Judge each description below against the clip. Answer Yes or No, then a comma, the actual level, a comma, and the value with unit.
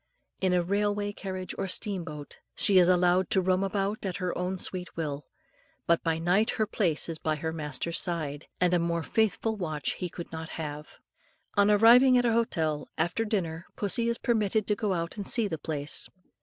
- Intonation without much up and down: No, average, 4.0 semitones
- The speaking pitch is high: No, medium, 180 Hz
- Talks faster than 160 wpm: Yes, average, 195 wpm